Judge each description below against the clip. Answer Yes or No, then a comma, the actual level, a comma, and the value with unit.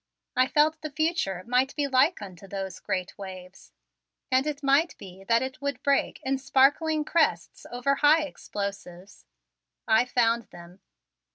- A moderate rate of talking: Yes, average, 150 wpm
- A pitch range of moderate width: No, wide, 6.7 semitones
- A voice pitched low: No, very high, 255 Hz